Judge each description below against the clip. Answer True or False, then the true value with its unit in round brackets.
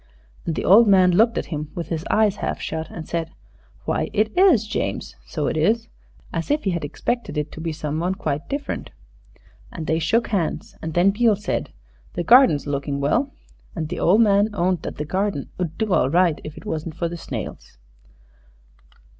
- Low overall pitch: False (175 Hz)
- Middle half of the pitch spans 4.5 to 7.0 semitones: True (5.2 semitones)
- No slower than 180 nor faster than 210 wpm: True (195 wpm)